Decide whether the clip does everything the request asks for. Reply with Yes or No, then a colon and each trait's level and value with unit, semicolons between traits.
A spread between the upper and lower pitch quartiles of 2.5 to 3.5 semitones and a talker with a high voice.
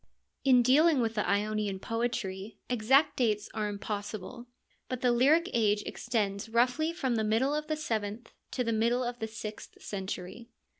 Yes: average, 3.1 semitones; high, 230 Hz